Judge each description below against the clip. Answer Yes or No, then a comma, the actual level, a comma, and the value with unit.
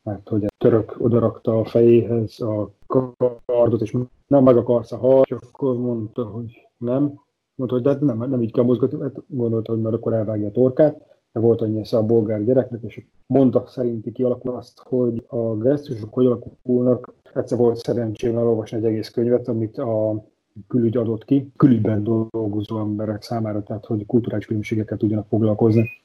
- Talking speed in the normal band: No, fast, 175 wpm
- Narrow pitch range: Yes, narrow, 2.1 semitones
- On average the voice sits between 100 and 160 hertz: Yes, low, 120 Hz